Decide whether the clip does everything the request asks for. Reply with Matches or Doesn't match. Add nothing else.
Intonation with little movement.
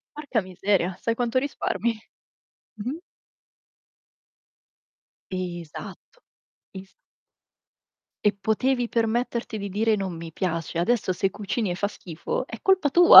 Doesn't match